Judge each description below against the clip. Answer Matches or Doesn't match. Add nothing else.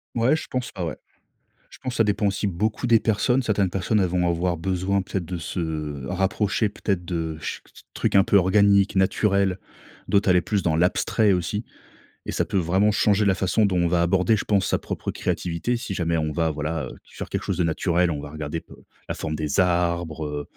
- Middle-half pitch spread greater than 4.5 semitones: Doesn't match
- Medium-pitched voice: Doesn't match